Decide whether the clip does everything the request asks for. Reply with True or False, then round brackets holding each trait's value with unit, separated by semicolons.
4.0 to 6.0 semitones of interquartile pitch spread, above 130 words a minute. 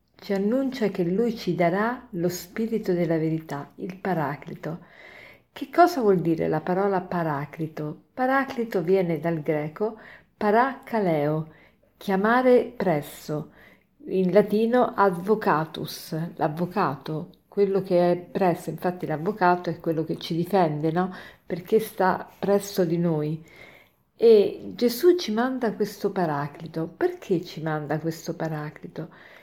False (4.7 semitones; 120 wpm)